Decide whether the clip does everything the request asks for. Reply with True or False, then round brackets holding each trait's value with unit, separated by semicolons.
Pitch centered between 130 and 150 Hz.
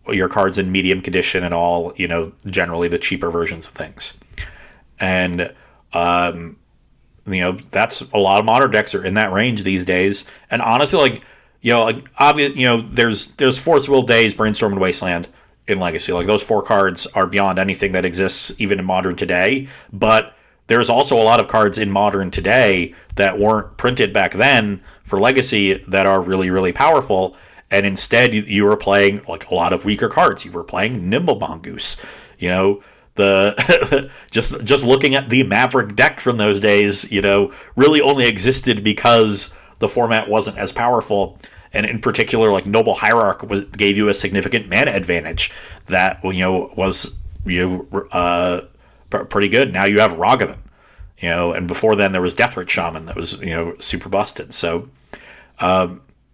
False (100 Hz)